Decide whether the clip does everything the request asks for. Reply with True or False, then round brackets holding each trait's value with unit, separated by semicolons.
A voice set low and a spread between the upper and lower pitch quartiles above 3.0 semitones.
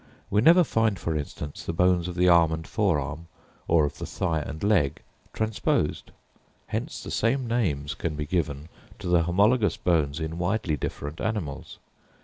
True (85 Hz; 5.1 semitones)